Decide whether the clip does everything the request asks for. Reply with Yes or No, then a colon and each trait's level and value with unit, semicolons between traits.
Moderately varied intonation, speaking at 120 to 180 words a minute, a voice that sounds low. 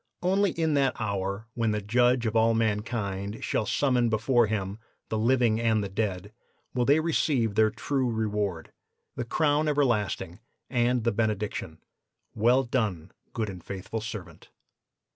Yes: average, 3.3 semitones; average, 145 wpm; low, 110 Hz